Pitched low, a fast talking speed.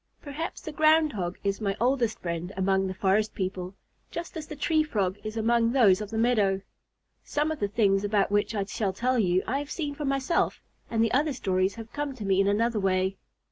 No: high, 215 Hz; fast, 220 wpm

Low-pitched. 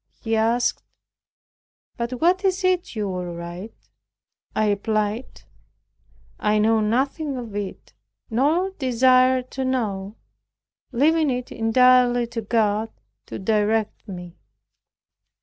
No: high, 230 Hz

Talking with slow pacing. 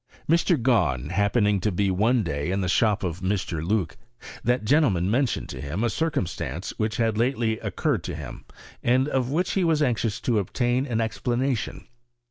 No: average, 175 wpm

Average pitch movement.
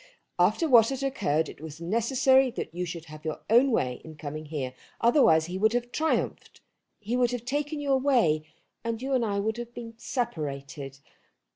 No: wide, 8.1 semitones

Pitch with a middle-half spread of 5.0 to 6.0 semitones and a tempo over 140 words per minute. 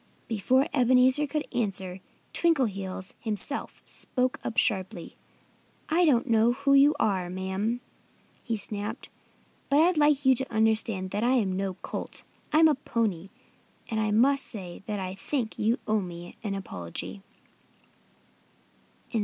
No: average, 5.3 semitones; slow, 135 wpm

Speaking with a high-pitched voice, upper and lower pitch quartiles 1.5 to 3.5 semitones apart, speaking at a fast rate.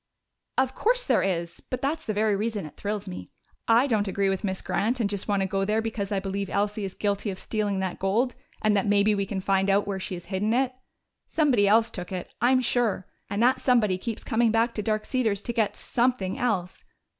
Yes: high, 210 Hz; average, 3.0 semitones; fast, 225 wpm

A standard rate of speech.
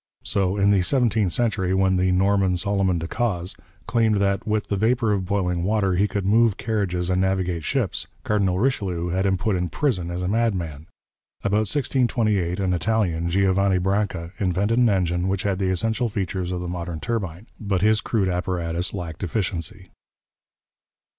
Yes: average, 170 wpm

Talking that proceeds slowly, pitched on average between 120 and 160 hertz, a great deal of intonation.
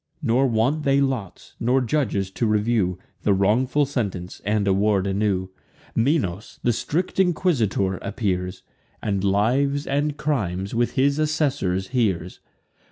No: slow, 130 wpm; low, 110 Hz; wide, 6.0 semitones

